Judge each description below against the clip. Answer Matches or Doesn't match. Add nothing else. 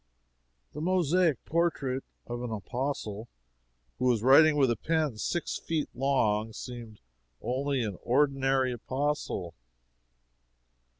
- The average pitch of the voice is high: Doesn't match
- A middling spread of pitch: Matches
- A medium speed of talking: Doesn't match